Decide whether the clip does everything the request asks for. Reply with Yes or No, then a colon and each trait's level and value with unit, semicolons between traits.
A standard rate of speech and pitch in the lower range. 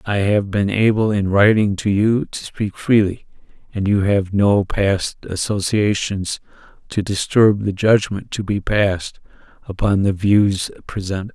Yes: average, 150 wpm; low, 100 Hz